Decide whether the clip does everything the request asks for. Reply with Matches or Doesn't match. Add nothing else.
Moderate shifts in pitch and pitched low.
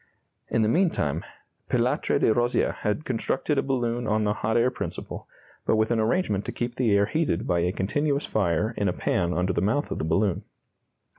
Matches